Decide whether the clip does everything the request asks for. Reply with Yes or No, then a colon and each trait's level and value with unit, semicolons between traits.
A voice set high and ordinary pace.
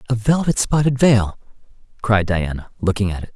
No: low, 110 Hz; average, 160 wpm